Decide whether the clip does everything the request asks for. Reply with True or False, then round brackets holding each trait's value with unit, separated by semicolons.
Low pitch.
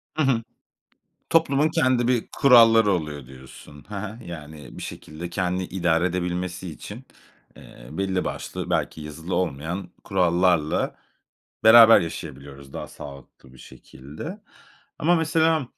True (90 Hz)